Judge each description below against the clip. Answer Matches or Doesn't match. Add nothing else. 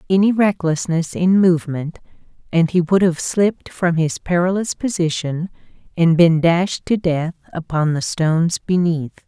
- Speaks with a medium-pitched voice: Matches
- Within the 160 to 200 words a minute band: Doesn't match